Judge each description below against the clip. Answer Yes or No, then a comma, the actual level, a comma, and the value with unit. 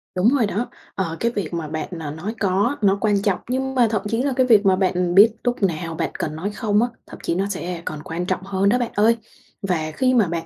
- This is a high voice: Yes, high, 195 Hz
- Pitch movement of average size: Yes, average, 4.7 semitones